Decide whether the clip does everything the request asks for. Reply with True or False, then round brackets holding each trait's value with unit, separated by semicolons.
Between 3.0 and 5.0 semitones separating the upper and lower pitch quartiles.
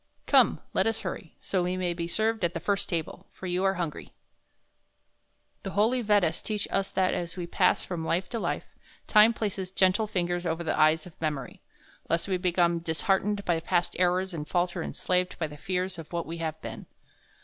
False (2.5 semitones)